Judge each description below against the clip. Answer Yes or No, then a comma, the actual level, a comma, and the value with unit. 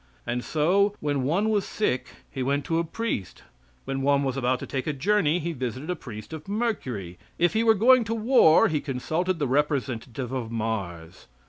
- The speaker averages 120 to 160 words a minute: No, average, 195 wpm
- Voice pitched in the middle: Yes, medium, 145 Hz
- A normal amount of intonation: No, wide, 6.7 semitones